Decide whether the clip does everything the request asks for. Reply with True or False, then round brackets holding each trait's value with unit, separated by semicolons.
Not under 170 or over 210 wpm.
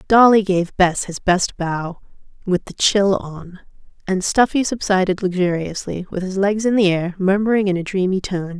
True (175 wpm)